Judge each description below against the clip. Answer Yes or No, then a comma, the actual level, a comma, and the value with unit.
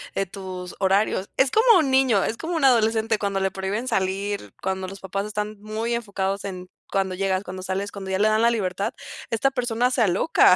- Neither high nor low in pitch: No, high, 200 Hz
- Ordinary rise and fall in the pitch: Yes, average, 3.2 semitones